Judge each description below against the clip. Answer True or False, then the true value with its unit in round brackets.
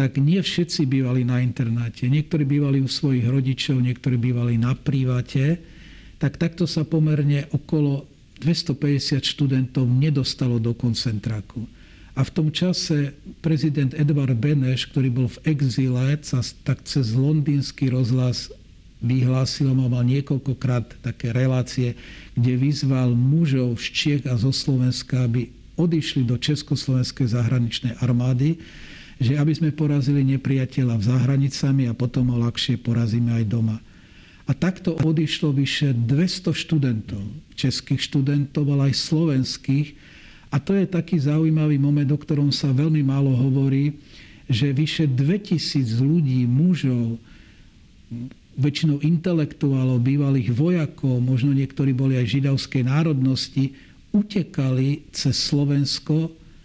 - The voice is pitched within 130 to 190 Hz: True (135 Hz)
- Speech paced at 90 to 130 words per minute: True (125 wpm)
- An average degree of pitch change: True (3.0 semitones)